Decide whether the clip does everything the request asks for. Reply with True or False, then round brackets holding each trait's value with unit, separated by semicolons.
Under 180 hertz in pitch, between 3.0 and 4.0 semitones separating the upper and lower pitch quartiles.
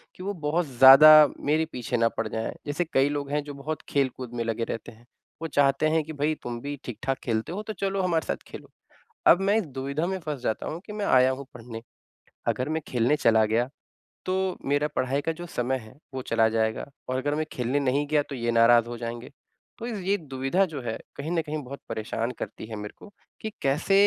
False (140 Hz; 4.7 semitones)